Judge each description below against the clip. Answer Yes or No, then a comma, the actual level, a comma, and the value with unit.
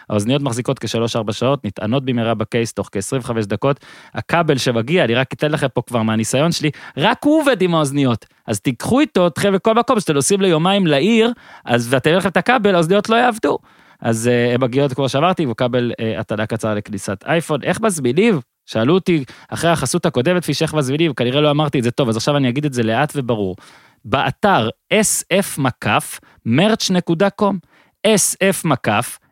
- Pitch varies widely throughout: Yes, wide, 7.0 semitones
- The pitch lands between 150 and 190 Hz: No, medium, 140 Hz